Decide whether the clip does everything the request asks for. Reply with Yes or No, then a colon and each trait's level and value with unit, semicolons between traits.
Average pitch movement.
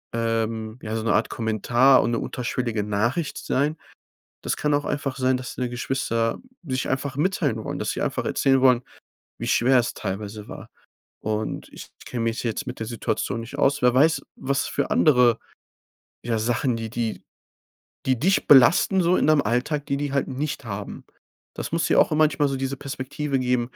Yes: average, 3.5 semitones